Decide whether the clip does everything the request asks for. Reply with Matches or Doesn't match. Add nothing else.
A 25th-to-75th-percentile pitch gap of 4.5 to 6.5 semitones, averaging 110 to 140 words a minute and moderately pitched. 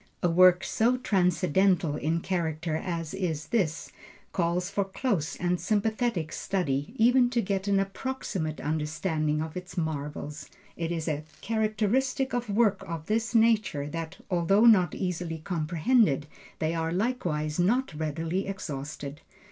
Matches